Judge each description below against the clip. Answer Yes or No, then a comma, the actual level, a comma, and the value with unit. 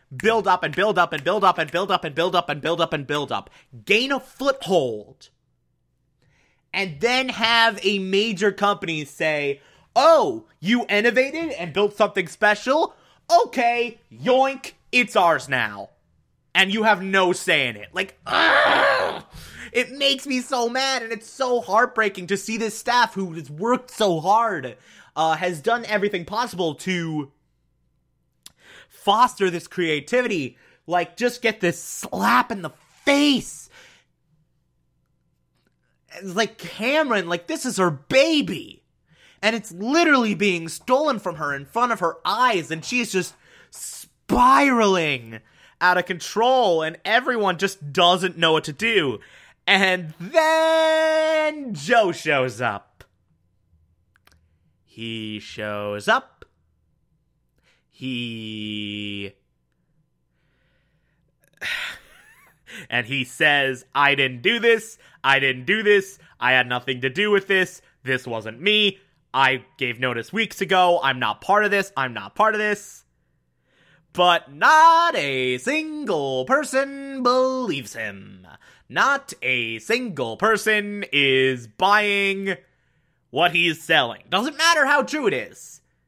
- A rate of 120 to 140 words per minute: Yes, slow, 135 wpm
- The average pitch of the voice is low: No, high, 190 Hz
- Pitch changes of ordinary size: No, wide, 8.8 semitones